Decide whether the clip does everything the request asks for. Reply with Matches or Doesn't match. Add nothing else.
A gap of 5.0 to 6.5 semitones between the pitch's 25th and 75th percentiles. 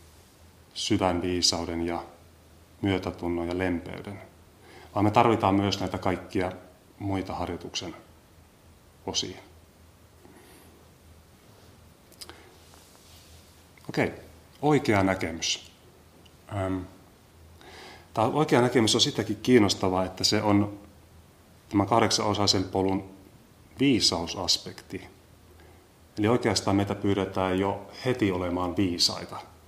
Doesn't match